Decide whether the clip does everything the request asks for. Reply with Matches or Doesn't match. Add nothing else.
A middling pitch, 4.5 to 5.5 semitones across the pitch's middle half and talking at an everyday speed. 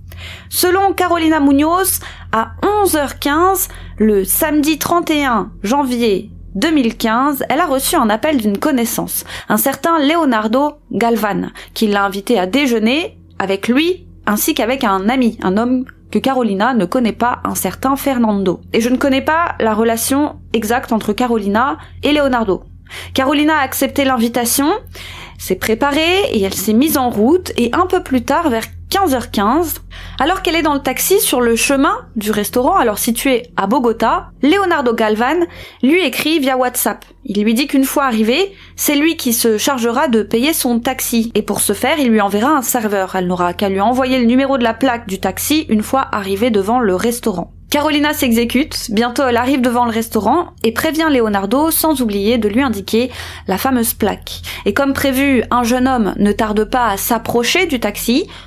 Doesn't match